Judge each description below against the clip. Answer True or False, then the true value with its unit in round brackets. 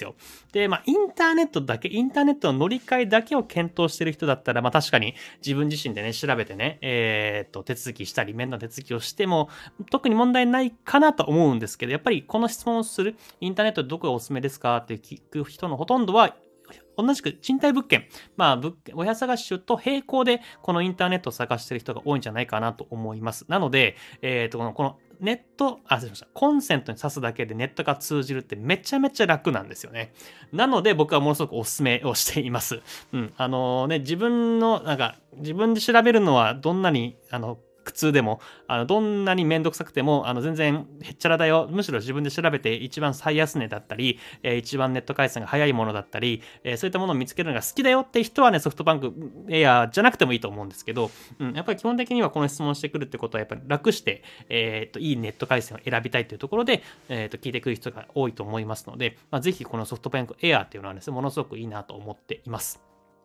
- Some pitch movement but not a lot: False (7.7 semitones)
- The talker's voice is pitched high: False (145 Hz)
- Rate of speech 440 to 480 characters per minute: True (470 characters per minute)